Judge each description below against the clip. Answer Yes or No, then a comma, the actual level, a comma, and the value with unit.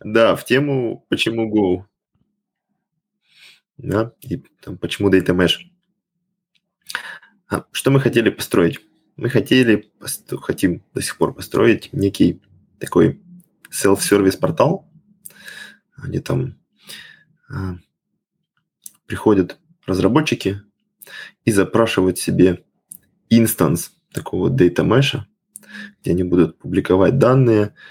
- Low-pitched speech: Yes, low, 115 Hz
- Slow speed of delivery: Yes, slow, 95 wpm